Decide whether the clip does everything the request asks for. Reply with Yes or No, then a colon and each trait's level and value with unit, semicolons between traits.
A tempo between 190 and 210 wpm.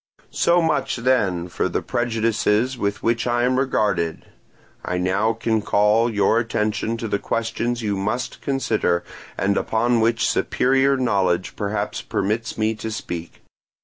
No: average, 145 wpm